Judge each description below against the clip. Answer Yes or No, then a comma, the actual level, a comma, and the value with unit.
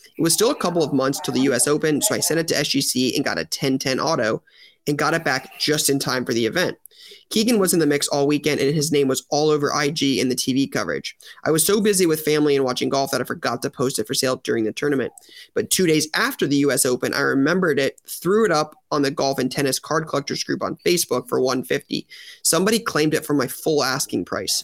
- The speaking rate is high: Yes, fast, 250 wpm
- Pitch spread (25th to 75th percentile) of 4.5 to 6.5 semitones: No, average, 2.7 semitones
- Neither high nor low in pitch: Yes, medium, 145 Hz